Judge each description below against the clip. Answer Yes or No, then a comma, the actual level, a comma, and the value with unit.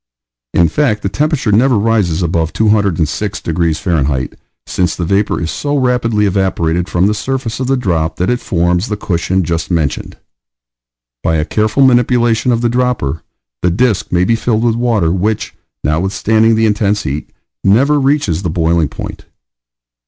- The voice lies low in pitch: Yes, low, 100 Hz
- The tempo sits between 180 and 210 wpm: No, average, 160 wpm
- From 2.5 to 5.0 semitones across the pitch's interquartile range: No, wide, 5.6 semitones